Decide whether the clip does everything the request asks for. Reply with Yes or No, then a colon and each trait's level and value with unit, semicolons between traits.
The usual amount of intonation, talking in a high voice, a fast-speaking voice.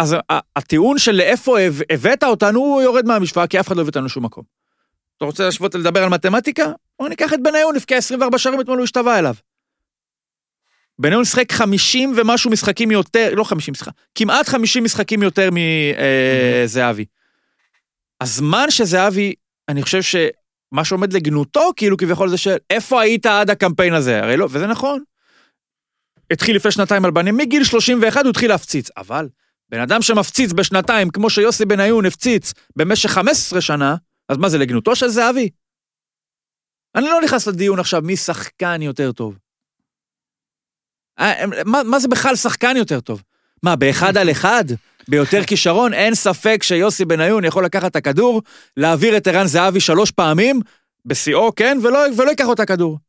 No: wide, 5.9 semitones; high, 200 Hz; fast, 160 wpm